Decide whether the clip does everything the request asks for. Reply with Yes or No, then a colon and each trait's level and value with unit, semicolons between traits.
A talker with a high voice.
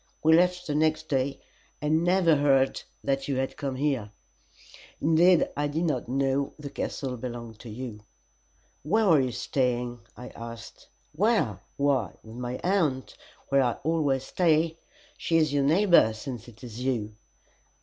No: medium, 140 Hz